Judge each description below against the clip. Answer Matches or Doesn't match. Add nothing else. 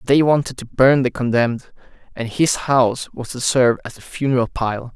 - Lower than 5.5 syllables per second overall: Matches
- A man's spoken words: Matches